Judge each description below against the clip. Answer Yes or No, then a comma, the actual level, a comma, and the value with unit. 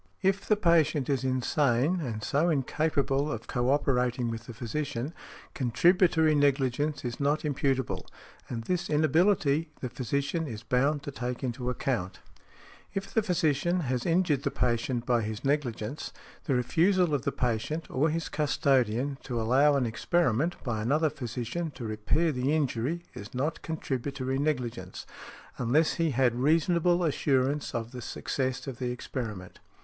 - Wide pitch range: No, average, 4.1 semitones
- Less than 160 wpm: Yes, average, 150 wpm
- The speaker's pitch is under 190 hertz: Yes, low, 135 Hz